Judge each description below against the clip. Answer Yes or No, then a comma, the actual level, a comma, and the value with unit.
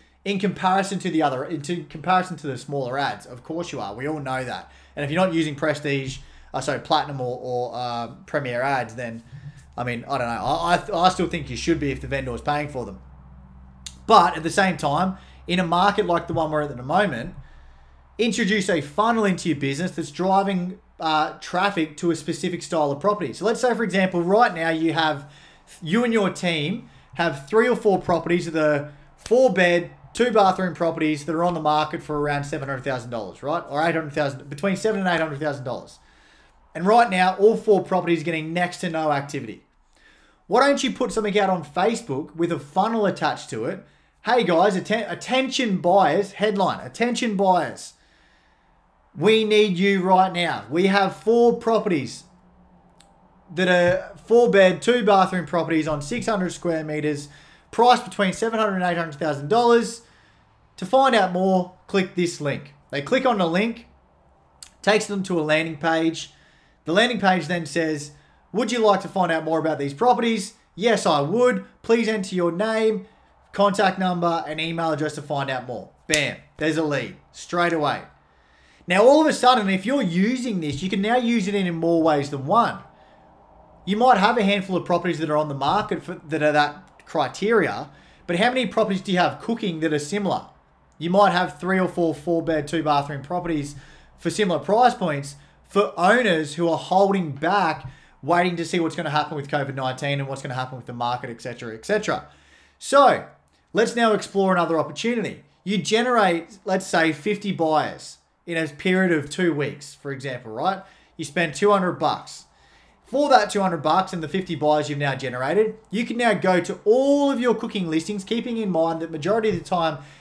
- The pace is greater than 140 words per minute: Yes, average, 190 wpm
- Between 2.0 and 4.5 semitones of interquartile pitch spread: No, average, 5.2 semitones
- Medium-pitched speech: Yes, medium, 175 Hz